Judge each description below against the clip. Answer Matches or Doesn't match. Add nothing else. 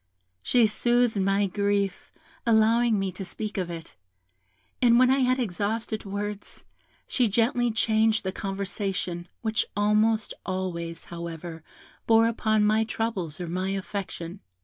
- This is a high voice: Matches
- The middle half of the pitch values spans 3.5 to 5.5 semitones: Doesn't match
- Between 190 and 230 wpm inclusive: Doesn't match